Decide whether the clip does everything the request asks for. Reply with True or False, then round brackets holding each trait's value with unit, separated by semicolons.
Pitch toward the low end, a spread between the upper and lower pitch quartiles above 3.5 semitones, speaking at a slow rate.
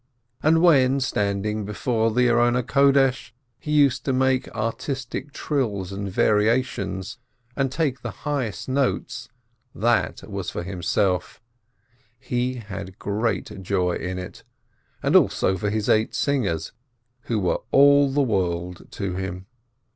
True (115 Hz; 5.1 semitones; 130 wpm)